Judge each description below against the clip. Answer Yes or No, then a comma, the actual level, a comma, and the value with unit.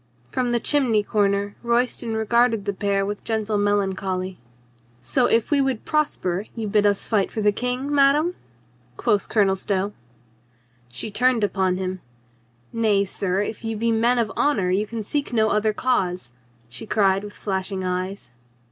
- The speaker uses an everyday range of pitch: Yes, average, 3.3 semitones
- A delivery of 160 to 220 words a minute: Yes, average, 165 wpm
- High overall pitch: Yes, high, 210 Hz